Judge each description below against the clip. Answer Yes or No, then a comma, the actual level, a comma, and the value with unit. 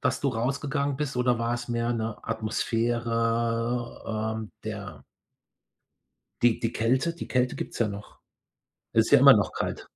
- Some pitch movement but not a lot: No, narrow, 1.9 semitones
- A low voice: Yes, low, 115 Hz